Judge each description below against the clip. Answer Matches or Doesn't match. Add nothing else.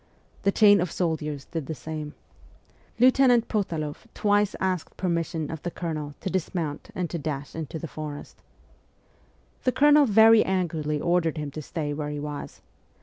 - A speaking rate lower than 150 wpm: Doesn't match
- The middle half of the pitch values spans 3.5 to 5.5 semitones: Matches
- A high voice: Doesn't match